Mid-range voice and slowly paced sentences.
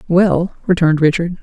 Yes: medium, 170 Hz; slow, 125 wpm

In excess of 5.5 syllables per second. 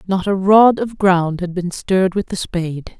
No: 4.6 syllables/s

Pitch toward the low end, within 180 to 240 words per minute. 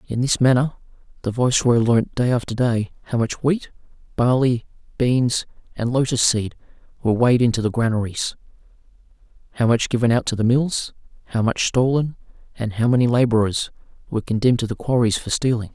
No: low, 120 Hz; average, 165 wpm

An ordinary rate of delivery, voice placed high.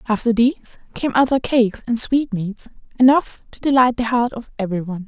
Yes: average, 175 wpm; high, 235 Hz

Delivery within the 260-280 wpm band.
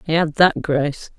No: average, 200 wpm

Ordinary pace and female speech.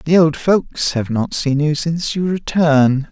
No: average, 190 wpm; male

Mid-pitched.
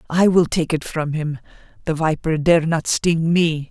Yes: medium, 160 Hz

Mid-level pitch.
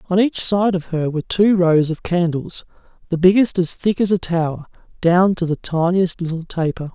Yes: medium, 175 Hz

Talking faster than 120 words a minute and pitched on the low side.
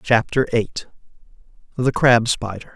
No: slow, 110 wpm; low, 120 Hz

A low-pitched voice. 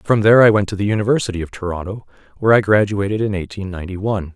Yes: low, 100 Hz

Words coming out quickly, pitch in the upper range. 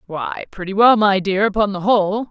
Yes: fast, 210 wpm; high, 200 Hz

